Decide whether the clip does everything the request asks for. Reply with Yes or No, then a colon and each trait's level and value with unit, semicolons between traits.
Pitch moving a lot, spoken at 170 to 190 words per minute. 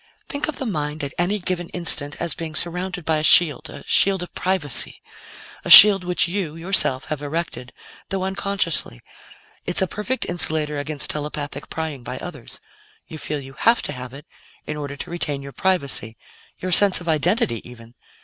No: average, 4.2 semitones; average, 180 wpm